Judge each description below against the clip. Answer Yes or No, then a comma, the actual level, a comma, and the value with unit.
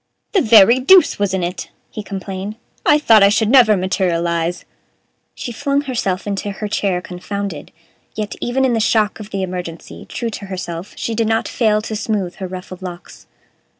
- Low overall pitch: No, high, 205 Hz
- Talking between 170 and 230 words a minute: Yes, average, 180 wpm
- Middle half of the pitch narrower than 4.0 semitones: Yes, average, 3.4 semitones